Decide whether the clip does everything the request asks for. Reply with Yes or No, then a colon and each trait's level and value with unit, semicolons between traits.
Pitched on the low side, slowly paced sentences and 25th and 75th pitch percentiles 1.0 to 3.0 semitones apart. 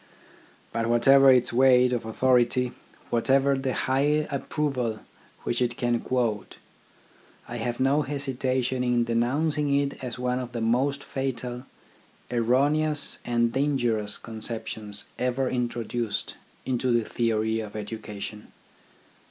Yes: low, 125 Hz; slow, 120 wpm; narrow, 2.4 semitones